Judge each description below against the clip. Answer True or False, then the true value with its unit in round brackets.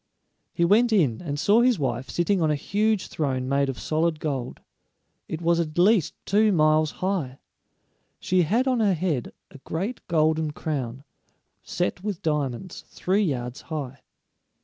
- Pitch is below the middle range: False (160 Hz)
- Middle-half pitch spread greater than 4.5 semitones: True (5.3 semitones)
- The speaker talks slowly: False (155 wpm)